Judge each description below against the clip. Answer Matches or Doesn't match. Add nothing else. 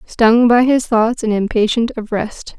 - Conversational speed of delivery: Matches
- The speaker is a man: Doesn't match